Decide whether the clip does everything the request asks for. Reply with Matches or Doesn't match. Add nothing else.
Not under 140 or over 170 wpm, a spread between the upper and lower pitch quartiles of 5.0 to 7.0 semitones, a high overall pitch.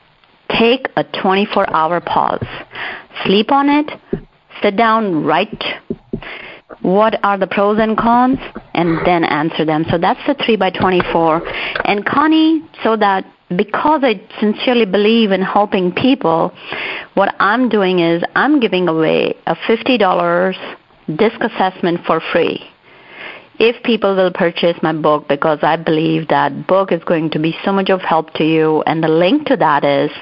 Matches